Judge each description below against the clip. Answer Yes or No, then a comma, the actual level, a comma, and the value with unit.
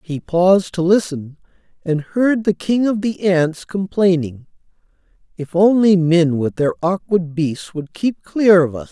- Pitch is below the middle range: No, medium, 180 Hz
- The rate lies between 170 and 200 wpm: No, average, 160 wpm